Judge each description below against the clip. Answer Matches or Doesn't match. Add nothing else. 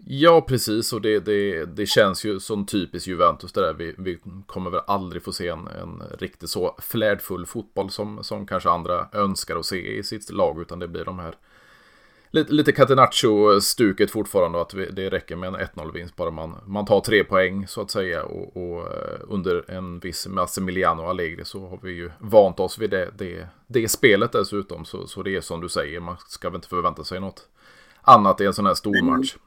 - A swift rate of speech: Matches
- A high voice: Doesn't match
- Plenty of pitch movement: Doesn't match